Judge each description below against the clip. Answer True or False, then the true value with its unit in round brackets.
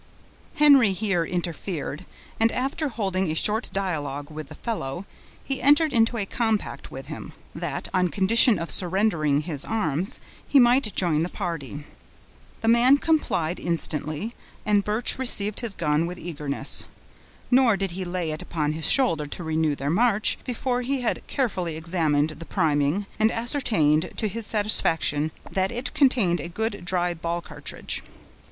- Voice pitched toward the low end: False (185 Hz)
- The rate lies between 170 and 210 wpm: False (155 wpm)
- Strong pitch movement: True (6.2 semitones)